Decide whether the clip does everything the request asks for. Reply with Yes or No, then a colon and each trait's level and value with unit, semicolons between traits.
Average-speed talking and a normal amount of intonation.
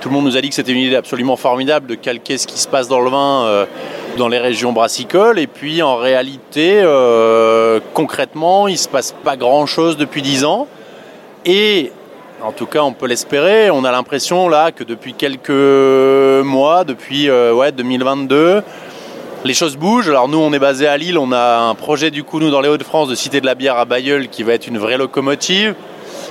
Yes: average, 210 wpm; average, 3.3 semitones